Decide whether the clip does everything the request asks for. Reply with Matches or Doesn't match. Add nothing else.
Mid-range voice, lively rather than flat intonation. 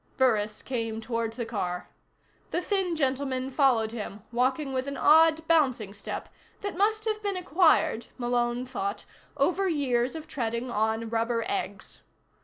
Doesn't match